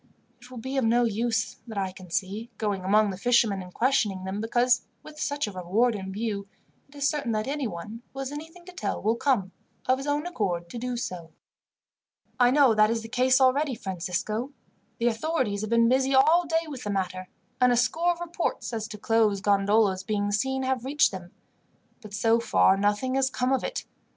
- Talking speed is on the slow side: No, fast, 205 wpm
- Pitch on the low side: No, high, 230 Hz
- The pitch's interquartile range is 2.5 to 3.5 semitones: No, average, 4.7 semitones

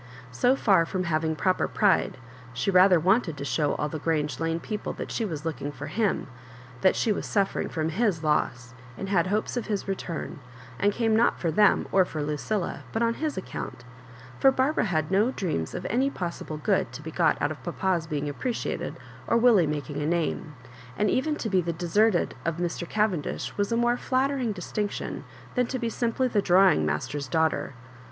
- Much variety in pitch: Yes, wide, 5.8 semitones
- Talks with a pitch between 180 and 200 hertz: Yes, medium, 185 Hz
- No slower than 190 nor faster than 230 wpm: Yes, average, 195 wpm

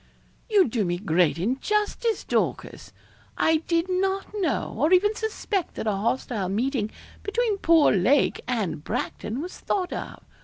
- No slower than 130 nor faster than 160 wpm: Yes, average, 145 wpm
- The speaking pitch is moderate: No, very high, 305 Hz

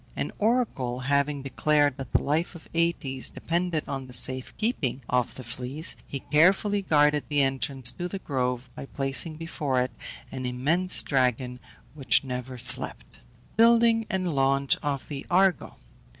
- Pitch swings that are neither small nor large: Yes, average, 4.6 semitones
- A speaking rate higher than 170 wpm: No, average, 150 wpm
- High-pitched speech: No, medium, 140 Hz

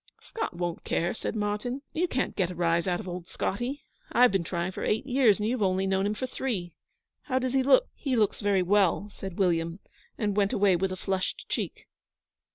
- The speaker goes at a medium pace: No, fast, 210 wpm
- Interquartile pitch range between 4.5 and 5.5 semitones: Yes, average, 5.1 semitones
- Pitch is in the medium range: No, high, 200 Hz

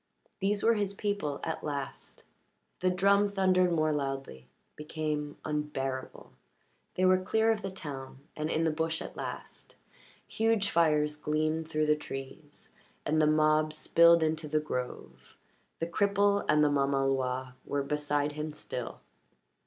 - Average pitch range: Yes, average, 3.9 semitones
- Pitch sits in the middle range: Yes, medium, 155 Hz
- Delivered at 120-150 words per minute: Yes, average, 145 wpm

